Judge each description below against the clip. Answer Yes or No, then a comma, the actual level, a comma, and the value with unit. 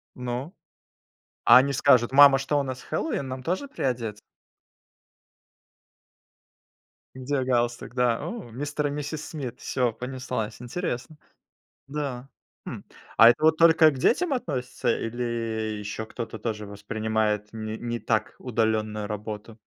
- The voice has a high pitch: No, low, 125 Hz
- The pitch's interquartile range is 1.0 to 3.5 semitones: No, average, 4.1 semitones